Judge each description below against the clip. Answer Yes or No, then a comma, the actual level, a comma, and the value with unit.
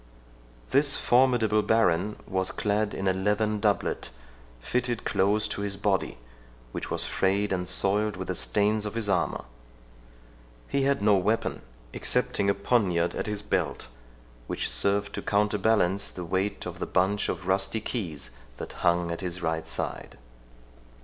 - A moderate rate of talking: Yes, average, 150 wpm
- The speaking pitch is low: Yes, low, 100 Hz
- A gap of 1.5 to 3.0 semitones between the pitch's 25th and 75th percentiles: Yes, narrow, 2.4 semitones